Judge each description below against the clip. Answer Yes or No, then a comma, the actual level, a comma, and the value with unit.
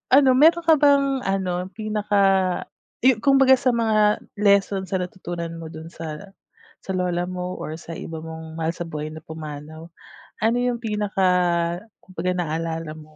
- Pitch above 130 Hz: Yes, medium, 185 Hz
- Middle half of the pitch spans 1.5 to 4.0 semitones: No, average, 5.0 semitones